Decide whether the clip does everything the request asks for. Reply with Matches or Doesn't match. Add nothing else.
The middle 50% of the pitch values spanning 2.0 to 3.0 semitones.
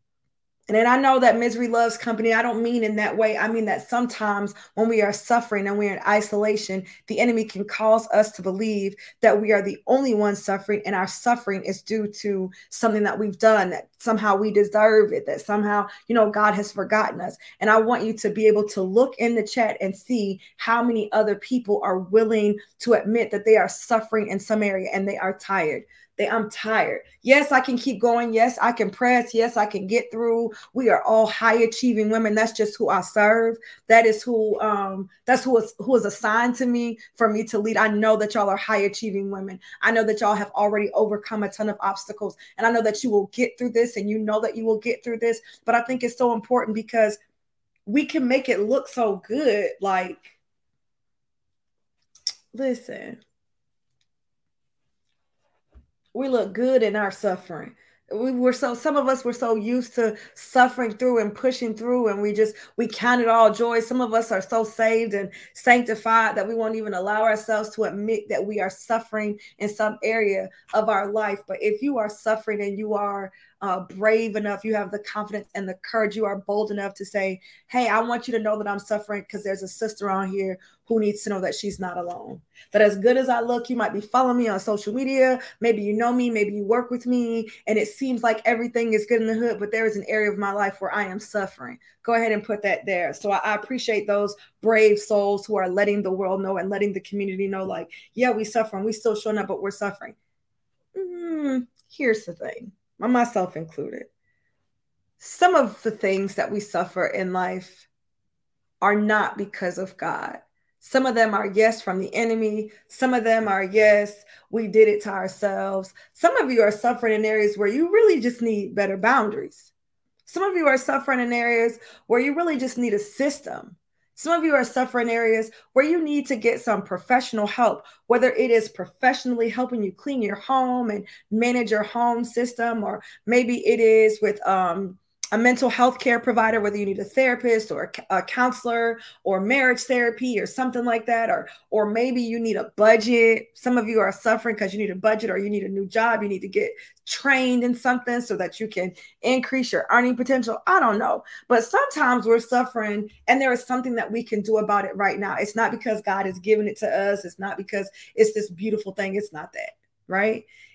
Matches